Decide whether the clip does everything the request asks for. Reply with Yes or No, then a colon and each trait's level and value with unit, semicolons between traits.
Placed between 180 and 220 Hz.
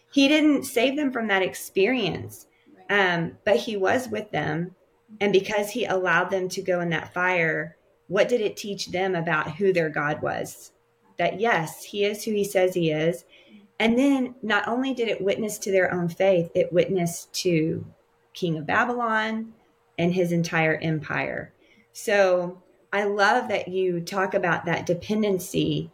Yes: high, 190 Hz